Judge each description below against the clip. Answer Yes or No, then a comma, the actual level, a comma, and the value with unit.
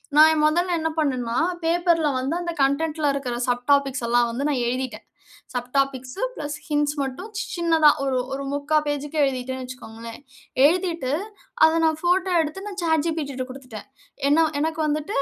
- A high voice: Yes, very high, 290 Hz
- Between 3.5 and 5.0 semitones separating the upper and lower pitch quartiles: Yes, average, 3.9 semitones